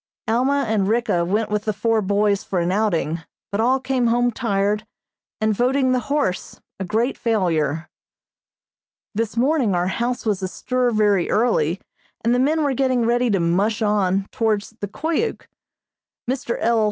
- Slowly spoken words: No, average, 160 wpm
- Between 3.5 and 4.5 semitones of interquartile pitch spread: Yes, average, 3.8 semitones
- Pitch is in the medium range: No, high, 220 Hz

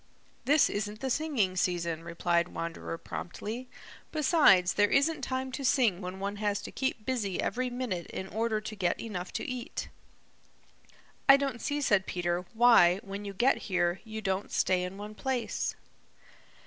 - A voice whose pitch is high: Yes, high, 210 Hz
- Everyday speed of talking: Yes, average, 160 wpm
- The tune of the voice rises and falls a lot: Yes, wide, 5.7 semitones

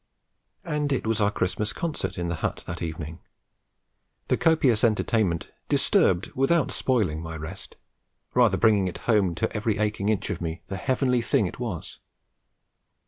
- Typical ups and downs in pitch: No, wide, 5.8 semitones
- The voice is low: Yes, low, 105 Hz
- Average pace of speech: Yes, average, 160 wpm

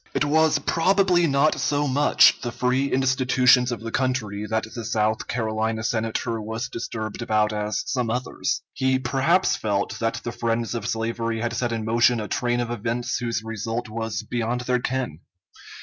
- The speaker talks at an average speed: Yes, average, 175 wpm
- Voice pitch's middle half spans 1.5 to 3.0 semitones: Yes, narrow, 2.5 semitones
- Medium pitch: No, low, 120 Hz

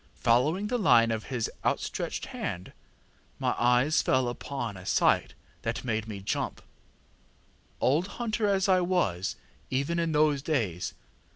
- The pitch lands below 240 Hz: Yes, low, 135 Hz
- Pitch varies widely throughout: Yes, wide, 7.3 semitones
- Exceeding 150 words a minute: No, slow, 135 wpm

